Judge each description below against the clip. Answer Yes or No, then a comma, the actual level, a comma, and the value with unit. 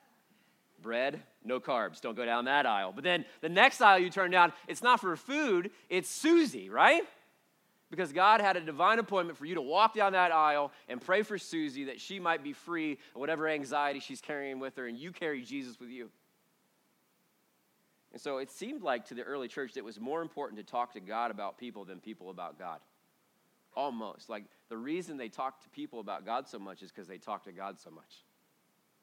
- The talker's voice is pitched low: No, medium, 160 Hz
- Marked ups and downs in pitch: Yes, wide, 6.8 semitones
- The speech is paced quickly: Yes, fast, 210 wpm